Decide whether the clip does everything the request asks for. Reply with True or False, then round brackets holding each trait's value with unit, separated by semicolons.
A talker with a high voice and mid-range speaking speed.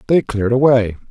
False (120 Hz; 165 wpm)